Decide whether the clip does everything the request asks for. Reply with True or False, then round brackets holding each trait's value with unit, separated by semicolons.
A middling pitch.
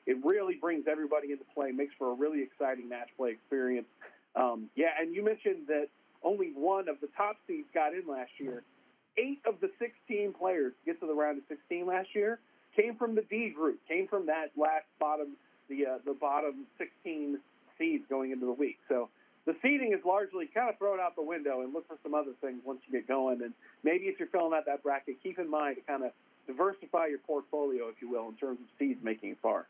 True (155 Hz)